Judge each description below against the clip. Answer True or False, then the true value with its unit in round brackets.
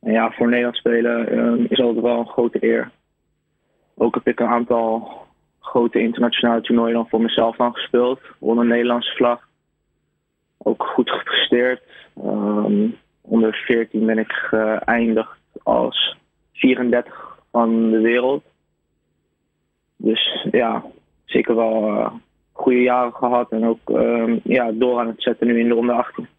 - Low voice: True (115 Hz)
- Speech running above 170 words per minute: False (145 wpm)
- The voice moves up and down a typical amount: False (1.3 semitones)